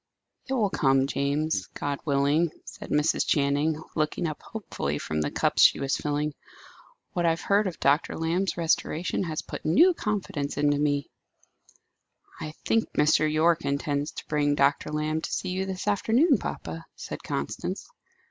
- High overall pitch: No, medium, 155 Hz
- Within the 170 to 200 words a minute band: No, average, 160 wpm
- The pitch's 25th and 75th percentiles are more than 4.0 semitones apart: No, average, 3.4 semitones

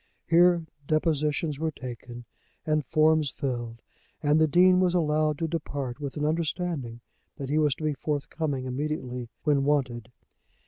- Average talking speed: Yes, average, 145 wpm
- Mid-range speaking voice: Yes, medium, 150 Hz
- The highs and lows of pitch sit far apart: No, average, 3.2 semitones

